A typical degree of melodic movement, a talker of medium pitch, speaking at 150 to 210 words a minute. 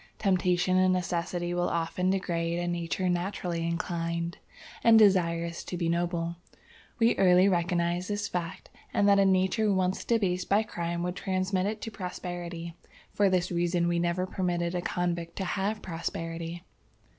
No: narrow, 1.7 semitones; medium, 180 Hz; average, 155 wpm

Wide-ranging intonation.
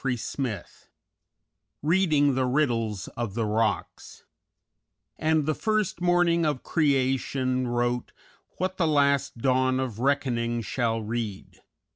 No: average, 4.3 semitones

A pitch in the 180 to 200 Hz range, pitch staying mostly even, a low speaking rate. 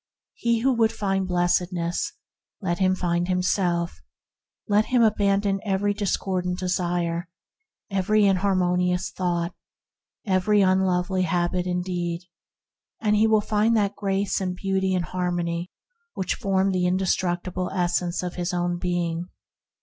Yes: medium, 185 Hz; narrow, 1.9 semitones; slow, 125 wpm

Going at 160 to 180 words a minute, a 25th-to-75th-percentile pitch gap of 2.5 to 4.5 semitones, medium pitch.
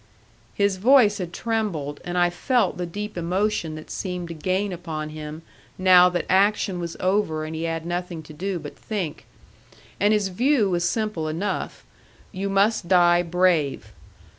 Yes: average, 165 wpm; average, 3.5 semitones; medium, 180 Hz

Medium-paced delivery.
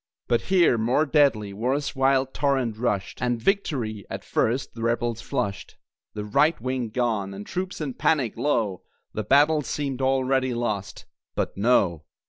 Yes: average, 150 wpm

